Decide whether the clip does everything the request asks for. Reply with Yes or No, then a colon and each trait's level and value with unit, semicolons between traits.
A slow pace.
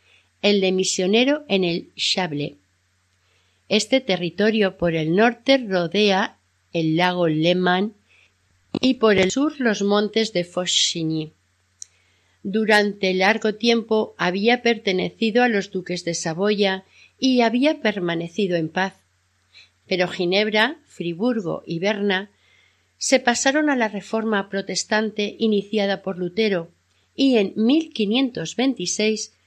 Yes: slow, 110 wpm